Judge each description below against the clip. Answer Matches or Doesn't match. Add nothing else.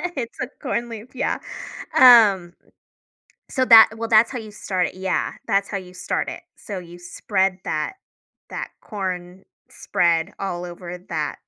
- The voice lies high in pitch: Matches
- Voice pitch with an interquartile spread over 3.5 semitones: Matches